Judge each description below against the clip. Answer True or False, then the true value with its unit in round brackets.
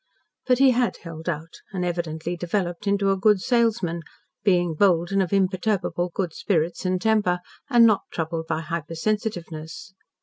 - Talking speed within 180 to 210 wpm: False (155 wpm)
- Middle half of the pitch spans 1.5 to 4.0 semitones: True (3.6 semitones)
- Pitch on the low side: False (180 Hz)